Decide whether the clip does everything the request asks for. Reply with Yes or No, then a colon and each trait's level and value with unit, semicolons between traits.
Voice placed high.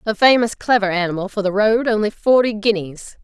Yes: high, 210 Hz